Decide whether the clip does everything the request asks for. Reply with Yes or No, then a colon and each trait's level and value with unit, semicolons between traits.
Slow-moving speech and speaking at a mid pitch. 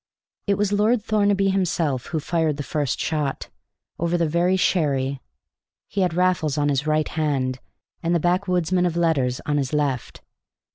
No: average, 160 wpm; medium, 160 Hz